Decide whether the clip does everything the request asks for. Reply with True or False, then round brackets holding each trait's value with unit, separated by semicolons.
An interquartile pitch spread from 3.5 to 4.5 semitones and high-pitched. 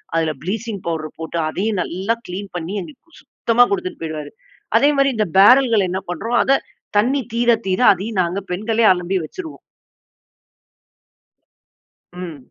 False (5.5 semitones; 205 Hz)